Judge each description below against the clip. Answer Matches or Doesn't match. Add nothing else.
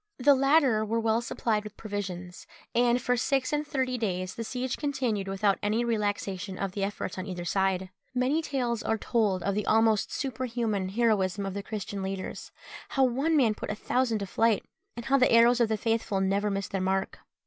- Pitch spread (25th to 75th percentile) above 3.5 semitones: Matches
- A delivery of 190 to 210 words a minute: Matches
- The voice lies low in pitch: Doesn't match